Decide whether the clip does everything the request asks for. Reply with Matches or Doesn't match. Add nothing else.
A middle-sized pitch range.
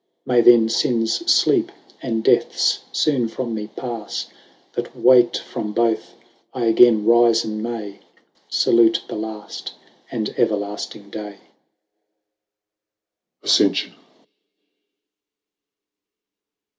Doesn't match